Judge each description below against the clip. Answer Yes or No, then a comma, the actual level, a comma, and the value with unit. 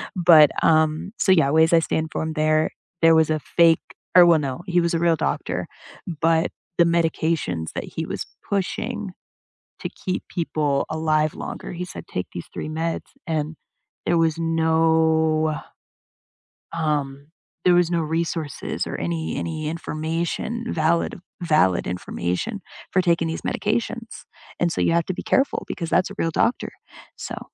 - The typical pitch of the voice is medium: Yes, medium, 160 Hz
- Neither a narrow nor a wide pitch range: No, narrow, 1.6 semitones